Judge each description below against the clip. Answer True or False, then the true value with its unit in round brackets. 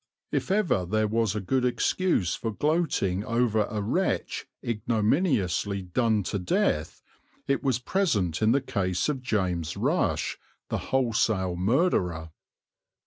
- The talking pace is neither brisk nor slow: False (130 wpm)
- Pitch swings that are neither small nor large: False (5.9 semitones)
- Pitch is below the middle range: True (110 Hz)